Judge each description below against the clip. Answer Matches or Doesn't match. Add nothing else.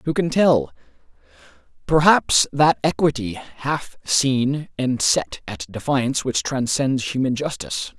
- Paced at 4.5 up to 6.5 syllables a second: Doesn't match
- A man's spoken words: Matches